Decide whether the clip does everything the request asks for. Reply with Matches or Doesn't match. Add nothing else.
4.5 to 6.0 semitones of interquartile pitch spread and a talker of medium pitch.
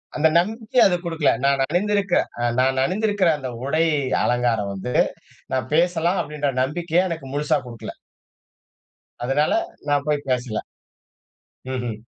Matches